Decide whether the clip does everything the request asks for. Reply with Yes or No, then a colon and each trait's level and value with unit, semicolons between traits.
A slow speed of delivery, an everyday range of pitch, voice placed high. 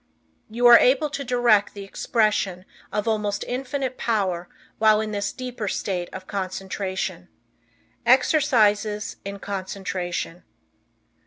Yes: slow, 110 wpm; average, 3.8 semitones; high, 210 Hz